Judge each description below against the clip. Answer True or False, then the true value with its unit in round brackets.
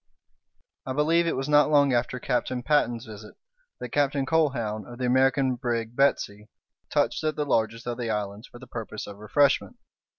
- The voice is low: True (125 Hz)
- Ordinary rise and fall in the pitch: True (3.8 semitones)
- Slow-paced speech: False (175 wpm)